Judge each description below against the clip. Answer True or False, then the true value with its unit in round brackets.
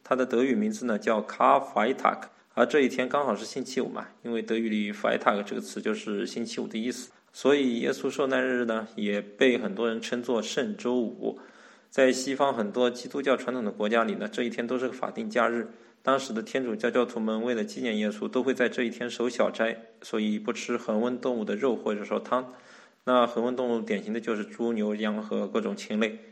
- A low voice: True (120 Hz)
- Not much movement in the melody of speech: True (2.1 semitones)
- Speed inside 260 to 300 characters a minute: False (335 characters per minute)